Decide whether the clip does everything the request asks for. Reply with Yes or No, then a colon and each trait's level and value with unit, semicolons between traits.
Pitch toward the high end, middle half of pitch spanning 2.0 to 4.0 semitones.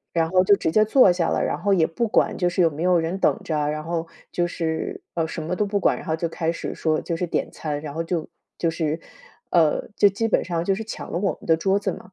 No: medium, 170 Hz; average, 3.0 semitones